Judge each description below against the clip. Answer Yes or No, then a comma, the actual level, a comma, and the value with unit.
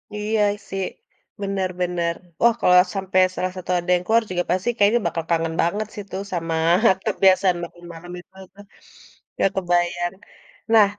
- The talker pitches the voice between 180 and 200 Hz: Yes, medium, 185 Hz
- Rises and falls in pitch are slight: Yes, narrow, 2.3 semitones